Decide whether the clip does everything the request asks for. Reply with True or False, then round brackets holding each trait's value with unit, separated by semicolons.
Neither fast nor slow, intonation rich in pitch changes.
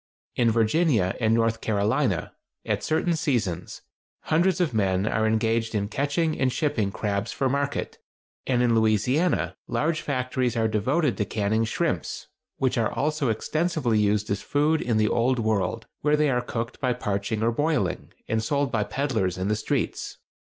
False (165 wpm; 4.9 semitones)